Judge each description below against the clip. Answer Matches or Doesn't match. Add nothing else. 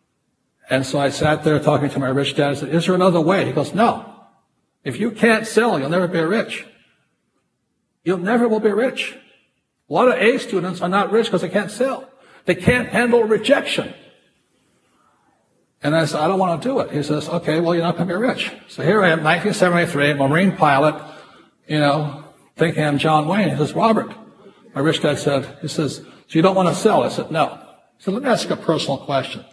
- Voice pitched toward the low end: Doesn't match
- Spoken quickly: Matches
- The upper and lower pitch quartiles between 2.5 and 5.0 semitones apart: Doesn't match